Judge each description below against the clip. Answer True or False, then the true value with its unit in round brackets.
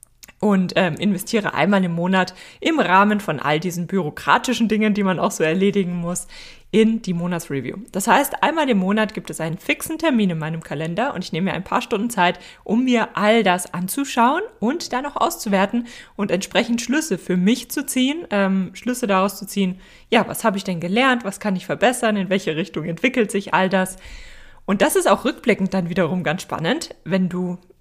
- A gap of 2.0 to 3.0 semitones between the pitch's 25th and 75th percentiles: False (4.2 semitones)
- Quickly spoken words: True (200 wpm)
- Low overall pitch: False (195 Hz)